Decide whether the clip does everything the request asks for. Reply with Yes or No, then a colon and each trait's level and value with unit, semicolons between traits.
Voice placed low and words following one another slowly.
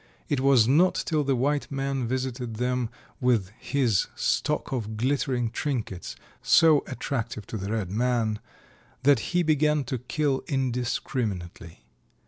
Yes: low, 125 Hz; slow, 130 wpm